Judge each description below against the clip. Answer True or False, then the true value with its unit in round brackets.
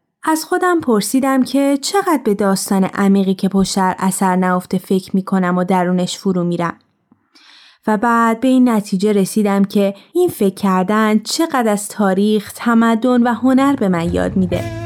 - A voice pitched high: True (205 Hz)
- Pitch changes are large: False (4.2 semitones)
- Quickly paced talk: True (160 wpm)